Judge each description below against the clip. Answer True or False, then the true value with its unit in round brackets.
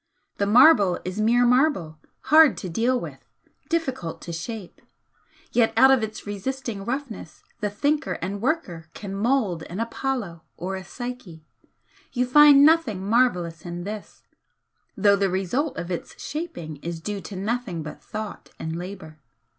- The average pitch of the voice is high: True (210 Hz)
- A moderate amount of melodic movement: False (6.1 semitones)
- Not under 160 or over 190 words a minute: False (150 wpm)